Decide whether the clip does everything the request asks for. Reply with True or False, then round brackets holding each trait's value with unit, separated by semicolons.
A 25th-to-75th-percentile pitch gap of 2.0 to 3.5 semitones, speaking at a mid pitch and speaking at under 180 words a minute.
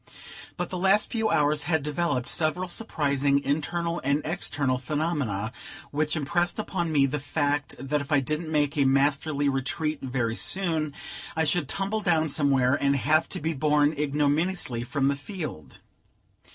True (2.8 semitones; 150 Hz; 155 wpm)